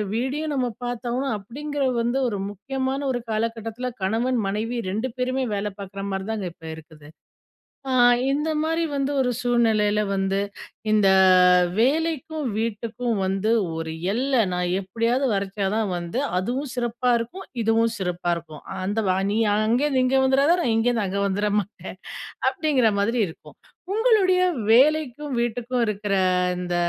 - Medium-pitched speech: No, high, 230 Hz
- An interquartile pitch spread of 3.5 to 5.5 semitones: Yes, average, 4.6 semitones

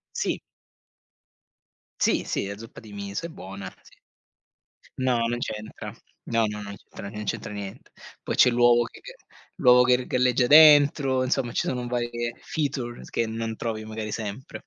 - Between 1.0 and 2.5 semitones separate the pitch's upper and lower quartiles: No, average, 2.9 semitones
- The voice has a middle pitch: No, low, 120 Hz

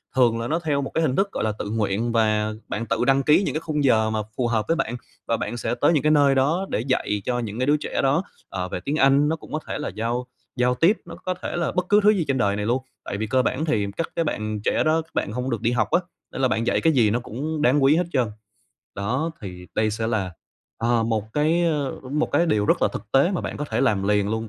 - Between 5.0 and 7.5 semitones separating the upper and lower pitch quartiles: Yes, wide, 5.5 semitones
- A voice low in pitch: Yes, low, 125 Hz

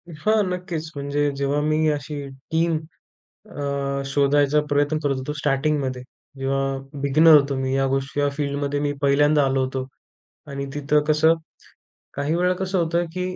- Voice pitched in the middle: Yes, medium, 145 Hz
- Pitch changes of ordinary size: No, narrow, 1.9 semitones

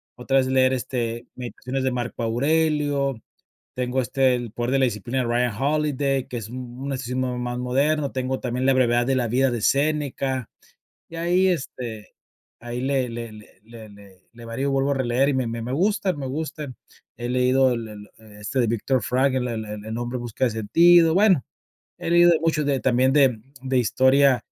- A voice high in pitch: No, low, 130 Hz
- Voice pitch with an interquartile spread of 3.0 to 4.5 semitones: No, narrow, 2.6 semitones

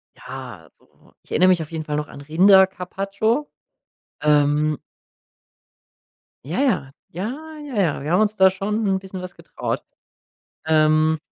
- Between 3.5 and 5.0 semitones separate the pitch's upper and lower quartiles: Yes, average, 4.5 semitones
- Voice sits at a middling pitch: Yes, medium, 180 Hz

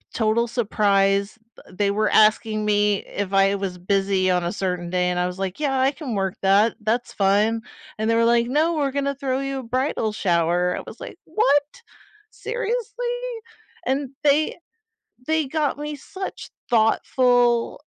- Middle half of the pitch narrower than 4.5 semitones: No, wide, 5.6 semitones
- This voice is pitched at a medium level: No, high, 220 Hz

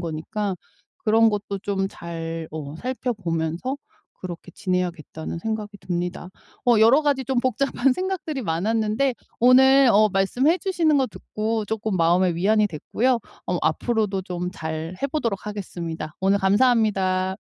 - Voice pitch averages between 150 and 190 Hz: No, high, 205 Hz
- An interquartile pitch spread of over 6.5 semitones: No, wide, 5.6 semitones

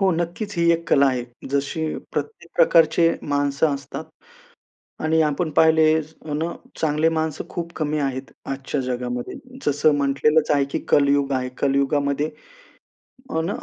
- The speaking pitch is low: No, medium, 150 Hz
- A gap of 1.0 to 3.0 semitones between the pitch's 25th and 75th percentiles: Yes, narrow, 2.5 semitones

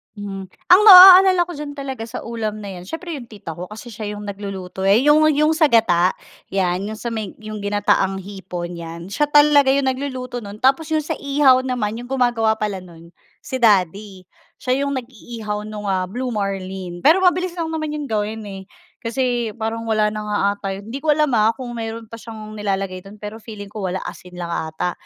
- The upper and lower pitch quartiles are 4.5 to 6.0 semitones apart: Yes, average, 5.1 semitones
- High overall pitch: Yes, high, 220 Hz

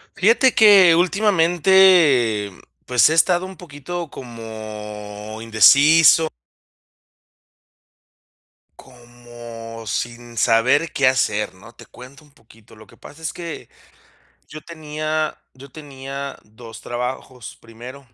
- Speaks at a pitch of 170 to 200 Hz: No, low, 130 Hz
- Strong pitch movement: Yes, wide, 6.0 semitones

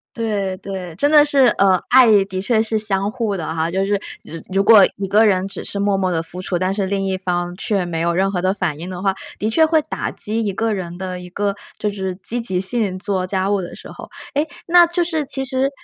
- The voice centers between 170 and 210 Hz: Yes, high, 195 Hz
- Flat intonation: No, average, 3.1 semitones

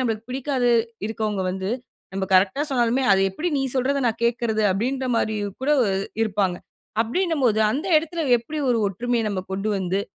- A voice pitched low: No, high, 230 Hz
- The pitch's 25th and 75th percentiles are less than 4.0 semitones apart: No, average, 4.8 semitones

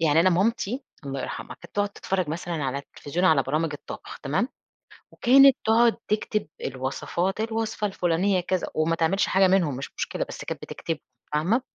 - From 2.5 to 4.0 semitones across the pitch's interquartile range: No, wide, 5.5 semitones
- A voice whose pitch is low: No, medium, 180 Hz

